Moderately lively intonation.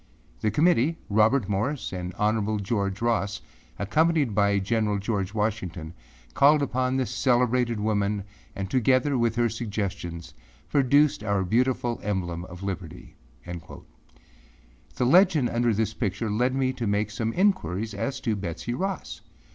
Yes: average, 4.3 semitones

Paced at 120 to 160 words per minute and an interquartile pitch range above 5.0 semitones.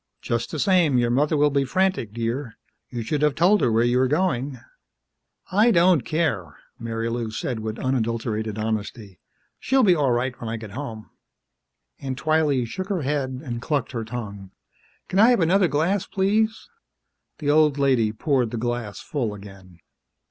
No: average, 170 wpm; wide, 5.5 semitones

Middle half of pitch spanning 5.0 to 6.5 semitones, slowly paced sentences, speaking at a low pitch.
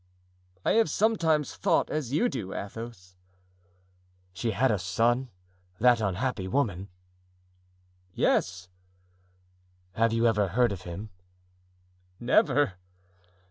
Yes: wide, 5.4 semitones; slow, 100 wpm; low, 115 Hz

